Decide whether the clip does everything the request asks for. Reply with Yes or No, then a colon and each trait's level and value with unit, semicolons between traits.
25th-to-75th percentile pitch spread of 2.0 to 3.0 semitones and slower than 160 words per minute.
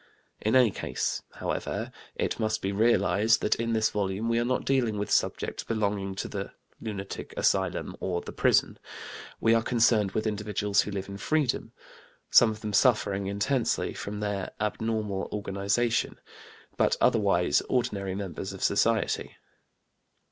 Yes: narrow, 2.4 semitones; average, 150 wpm